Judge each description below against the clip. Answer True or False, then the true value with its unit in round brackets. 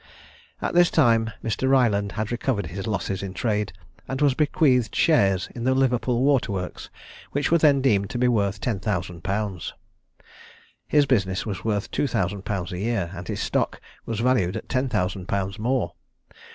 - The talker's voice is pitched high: False (110 Hz)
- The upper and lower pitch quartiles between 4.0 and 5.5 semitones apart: True (4.9 semitones)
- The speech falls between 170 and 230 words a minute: True (180 wpm)